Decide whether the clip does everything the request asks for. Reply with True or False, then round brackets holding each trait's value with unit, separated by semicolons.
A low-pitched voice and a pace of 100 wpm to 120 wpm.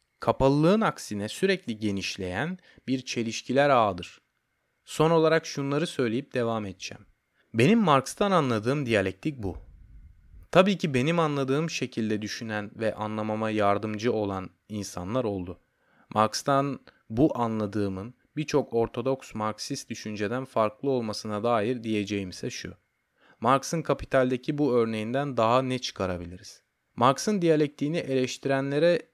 True (120 Hz; 105 wpm)